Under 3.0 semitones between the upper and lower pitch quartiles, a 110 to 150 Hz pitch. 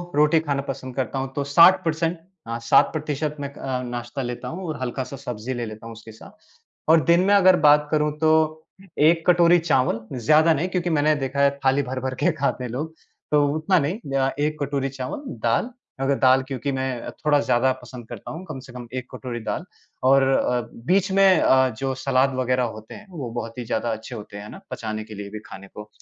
No: average, 4.1 semitones; low, 135 Hz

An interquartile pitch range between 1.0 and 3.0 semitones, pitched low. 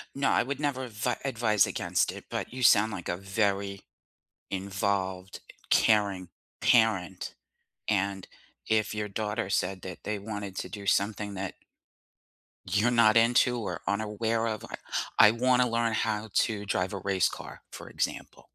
Yes: narrow, 2.6 semitones; low, 105 Hz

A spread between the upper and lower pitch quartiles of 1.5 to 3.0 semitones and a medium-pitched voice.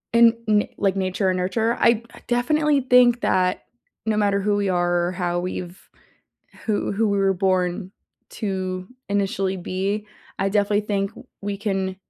No: narrow, 2.4 semitones; high, 195 Hz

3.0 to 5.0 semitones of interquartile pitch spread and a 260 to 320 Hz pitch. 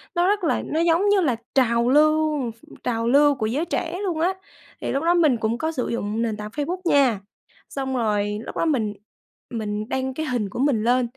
No: wide, 5.6 semitones; very high, 265 Hz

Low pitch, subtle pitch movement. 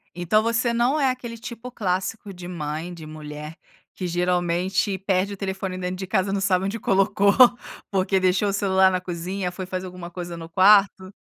No: high, 190 Hz; narrow, 2.1 semitones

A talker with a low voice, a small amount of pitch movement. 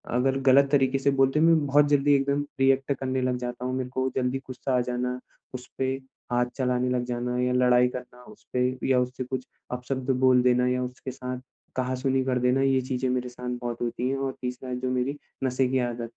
Yes: low, 125 Hz; narrow, 1.1 semitones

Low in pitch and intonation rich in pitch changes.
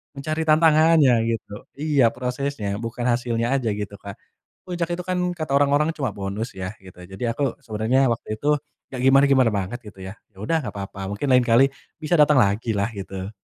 Yes: low, 120 Hz; wide, 5.8 semitones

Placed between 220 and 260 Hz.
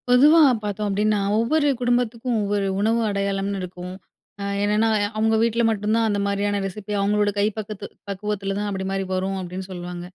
No: high, 205 Hz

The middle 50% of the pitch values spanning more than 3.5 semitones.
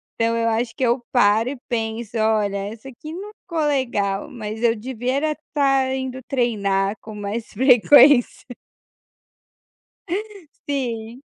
No: average, 3.2 semitones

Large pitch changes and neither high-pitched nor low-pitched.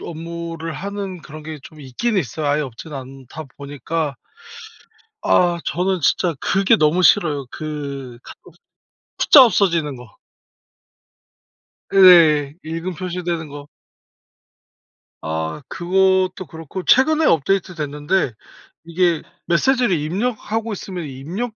No: average, 4.3 semitones; medium, 165 Hz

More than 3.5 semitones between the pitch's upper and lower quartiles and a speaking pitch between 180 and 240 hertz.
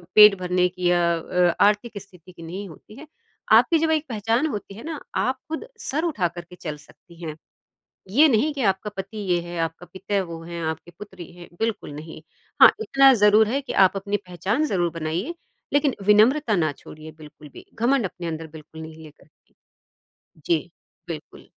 Yes: average, 5.2 semitones; high, 190 Hz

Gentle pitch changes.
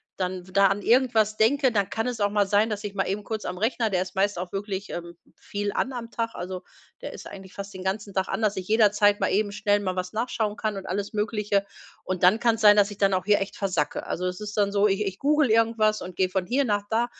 Yes: narrow, 2.2 semitones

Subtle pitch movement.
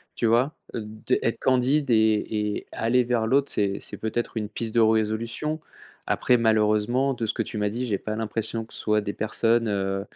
Yes: narrow, 1.9 semitones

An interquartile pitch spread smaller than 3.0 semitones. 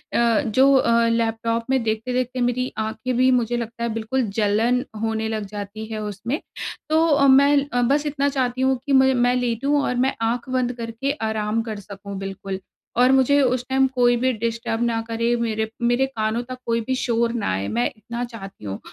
Yes: narrow, 2.6 semitones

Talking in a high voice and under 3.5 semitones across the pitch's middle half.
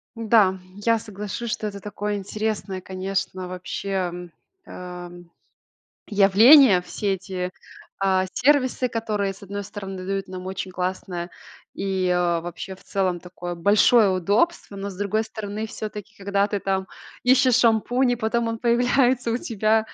Yes: high, 200 Hz; average, 2.9 semitones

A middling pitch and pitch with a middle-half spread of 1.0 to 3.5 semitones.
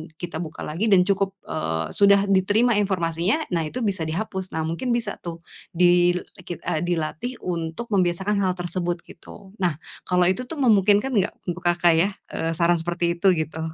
Yes: medium, 180 Hz; average, 3.0 semitones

